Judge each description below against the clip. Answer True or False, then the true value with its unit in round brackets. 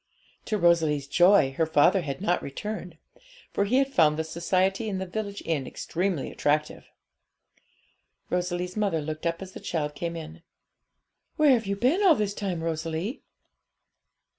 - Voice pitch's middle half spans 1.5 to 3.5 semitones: False (4.1 semitones)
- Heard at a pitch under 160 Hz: False (175 Hz)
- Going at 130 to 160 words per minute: True (155 wpm)